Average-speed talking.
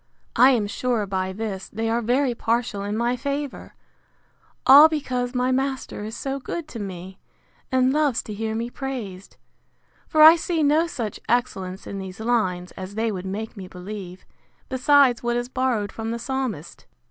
Yes: average, 170 wpm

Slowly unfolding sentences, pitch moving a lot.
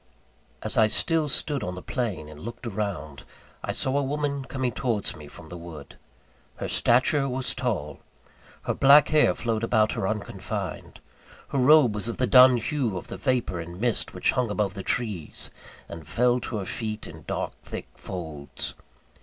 No: average, 180 wpm; wide, 6.1 semitones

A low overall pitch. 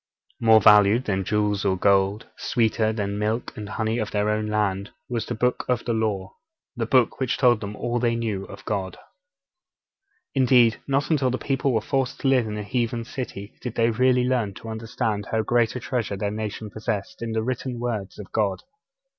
Yes: low, 110 Hz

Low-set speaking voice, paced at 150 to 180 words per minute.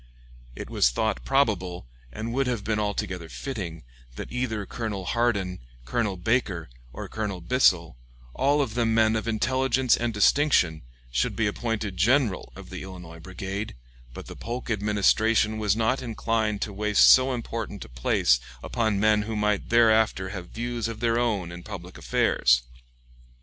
Yes: low, 110 Hz; average, 155 wpm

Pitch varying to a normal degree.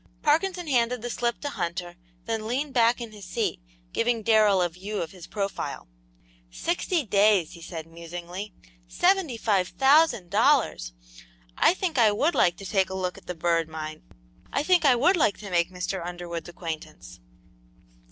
No: wide, 6.2 semitones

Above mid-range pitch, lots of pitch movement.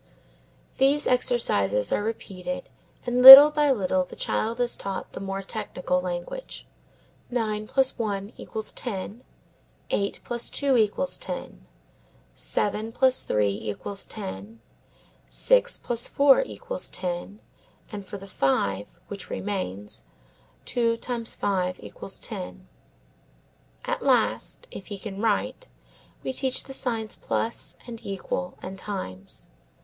No: high, 210 Hz; average, 4.8 semitones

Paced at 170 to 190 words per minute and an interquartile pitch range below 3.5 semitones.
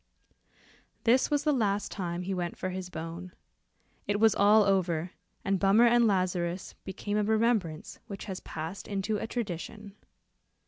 No: average, 155 wpm; average, 3.1 semitones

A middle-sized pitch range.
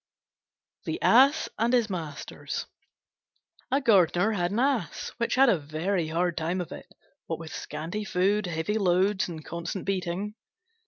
Yes: average, 4.0 semitones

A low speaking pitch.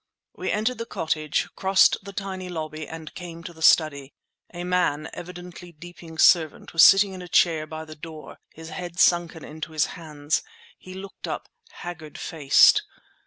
No: medium, 165 Hz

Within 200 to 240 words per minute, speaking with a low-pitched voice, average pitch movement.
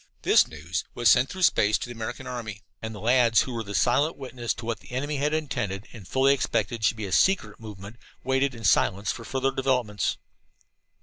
Yes: fast, 205 wpm; low, 120 Hz; average, 3.8 semitones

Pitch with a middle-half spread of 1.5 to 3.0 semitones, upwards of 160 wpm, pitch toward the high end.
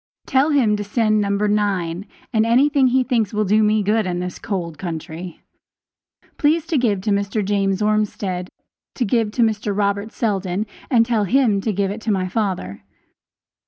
Yes: average, 2.7 semitones; average, 175 wpm; high, 210 Hz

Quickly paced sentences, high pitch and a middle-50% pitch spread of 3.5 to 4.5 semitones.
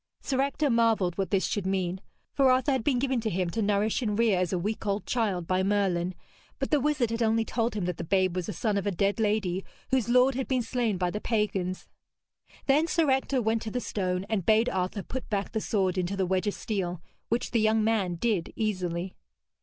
Yes: fast, 230 wpm; high, 210 Hz; average, 4.0 semitones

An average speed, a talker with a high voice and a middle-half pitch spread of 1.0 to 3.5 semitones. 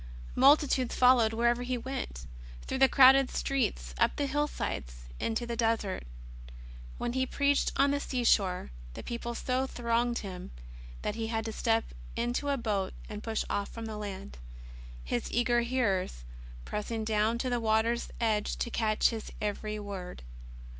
Yes: average, 155 wpm; high, 230 Hz; average, 3.0 semitones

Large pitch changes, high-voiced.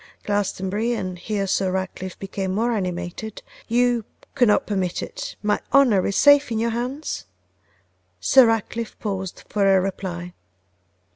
No: average, 3.7 semitones; high, 205 Hz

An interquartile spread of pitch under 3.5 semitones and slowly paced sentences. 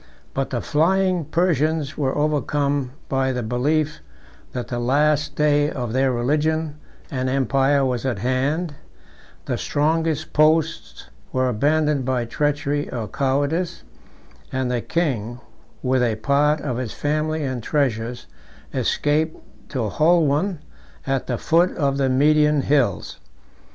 Yes: average, 3.0 semitones; slow, 130 wpm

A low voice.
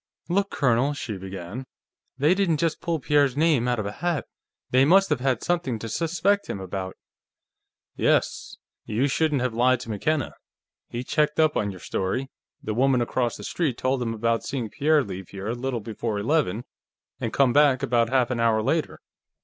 Yes: low, 125 Hz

